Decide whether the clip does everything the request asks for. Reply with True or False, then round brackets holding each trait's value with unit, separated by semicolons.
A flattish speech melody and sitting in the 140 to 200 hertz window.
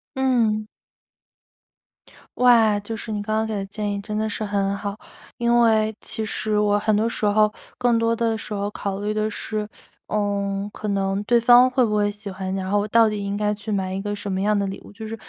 False (1.6 semitones; 210 Hz)